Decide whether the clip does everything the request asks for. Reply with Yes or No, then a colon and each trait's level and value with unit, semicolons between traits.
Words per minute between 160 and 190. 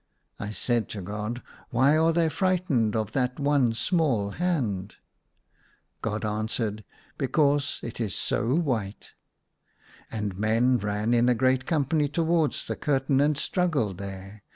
No: average, 150 wpm